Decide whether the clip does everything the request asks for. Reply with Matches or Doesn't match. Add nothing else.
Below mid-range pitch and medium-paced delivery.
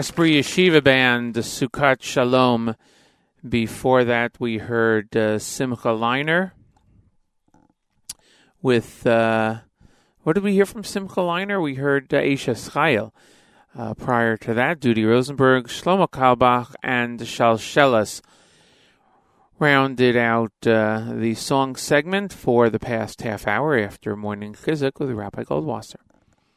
Doesn't match